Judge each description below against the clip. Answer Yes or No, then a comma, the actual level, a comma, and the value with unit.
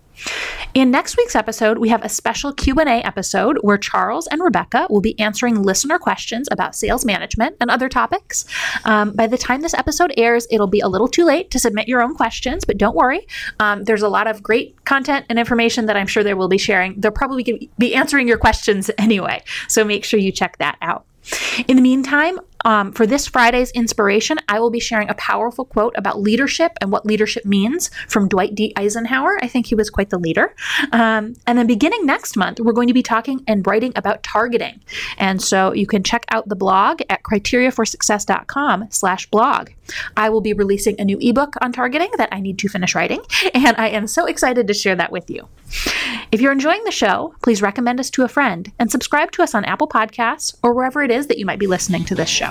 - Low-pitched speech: No, high, 230 Hz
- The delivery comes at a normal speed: No, fast, 215 wpm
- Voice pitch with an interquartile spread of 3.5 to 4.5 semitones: Yes, average, 3.8 semitones